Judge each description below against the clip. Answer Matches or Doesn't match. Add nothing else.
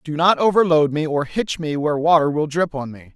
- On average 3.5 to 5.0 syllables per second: Doesn't match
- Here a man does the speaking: Matches